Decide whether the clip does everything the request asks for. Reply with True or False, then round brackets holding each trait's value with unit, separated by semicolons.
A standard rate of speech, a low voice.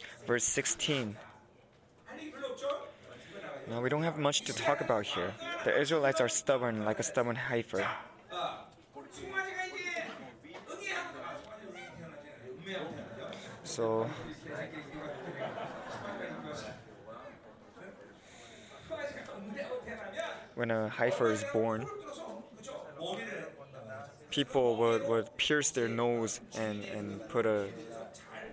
False (75 wpm; 130 Hz)